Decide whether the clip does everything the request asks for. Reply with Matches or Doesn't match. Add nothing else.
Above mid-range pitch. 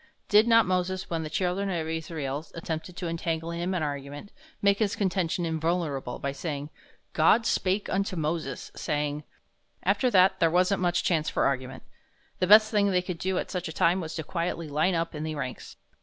Doesn't match